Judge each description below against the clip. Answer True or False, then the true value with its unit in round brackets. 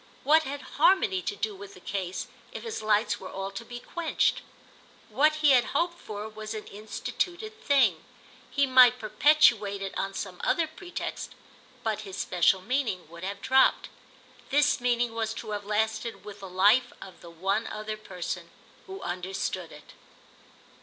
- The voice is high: True (215 Hz)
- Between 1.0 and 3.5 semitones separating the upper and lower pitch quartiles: False (5.4 semitones)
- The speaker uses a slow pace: False (165 wpm)